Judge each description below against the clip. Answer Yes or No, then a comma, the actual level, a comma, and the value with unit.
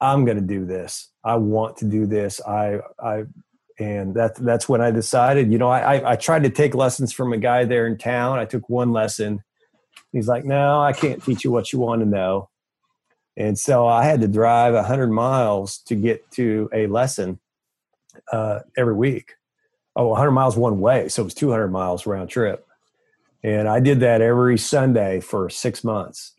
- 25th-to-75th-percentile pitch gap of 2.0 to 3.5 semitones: Yes, average, 3.2 semitones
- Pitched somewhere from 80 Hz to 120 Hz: Yes, low, 115 Hz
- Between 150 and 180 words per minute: No, average, 195 wpm